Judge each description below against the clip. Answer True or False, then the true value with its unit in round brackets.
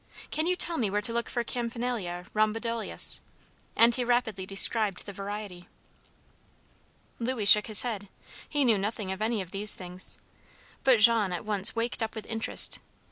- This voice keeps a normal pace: True (165 wpm)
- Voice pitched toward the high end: True (215 Hz)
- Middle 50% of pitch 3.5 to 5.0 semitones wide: False (3.0 semitones)